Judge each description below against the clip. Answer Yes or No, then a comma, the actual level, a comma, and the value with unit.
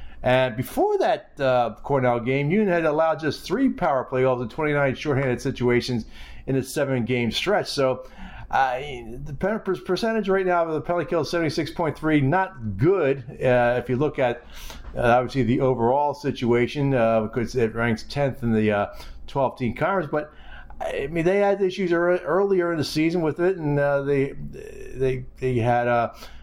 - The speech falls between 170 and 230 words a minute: Yes, average, 175 wpm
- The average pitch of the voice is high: No, low, 135 Hz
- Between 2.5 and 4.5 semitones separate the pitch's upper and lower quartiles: No, wide, 5.4 semitones